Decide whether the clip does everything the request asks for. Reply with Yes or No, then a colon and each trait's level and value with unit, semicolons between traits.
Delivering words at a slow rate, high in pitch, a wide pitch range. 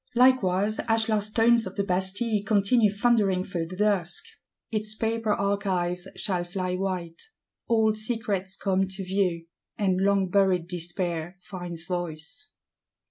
No: slow, 130 wpm; high, 195 Hz; average, 3.0 semitones